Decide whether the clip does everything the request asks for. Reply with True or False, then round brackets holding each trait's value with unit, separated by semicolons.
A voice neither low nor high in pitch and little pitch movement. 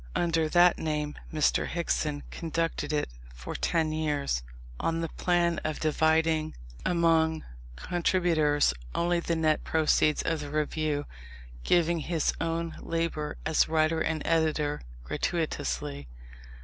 True (160 Hz; 1.7 semitones)